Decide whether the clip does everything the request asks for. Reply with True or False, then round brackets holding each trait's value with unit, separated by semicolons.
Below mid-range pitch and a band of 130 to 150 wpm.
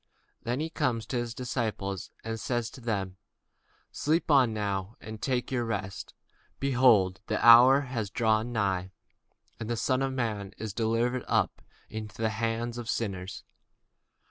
True (115 Hz; 145 wpm)